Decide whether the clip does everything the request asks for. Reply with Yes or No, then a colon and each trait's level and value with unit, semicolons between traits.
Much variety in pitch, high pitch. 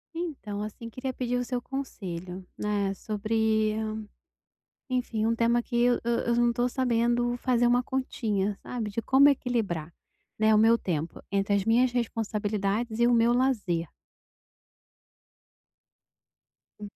No: average, 2.8 semitones; high, 230 Hz